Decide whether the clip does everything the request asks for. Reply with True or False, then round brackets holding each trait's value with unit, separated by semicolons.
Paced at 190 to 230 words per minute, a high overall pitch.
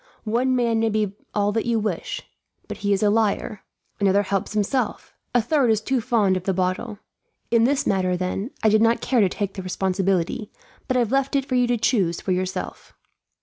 True (205 wpm; 215 Hz)